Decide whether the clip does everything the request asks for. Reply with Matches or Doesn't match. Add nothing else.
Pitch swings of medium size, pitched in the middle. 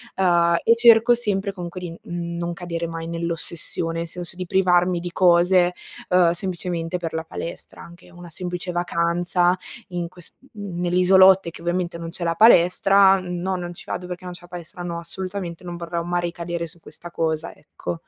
Doesn't match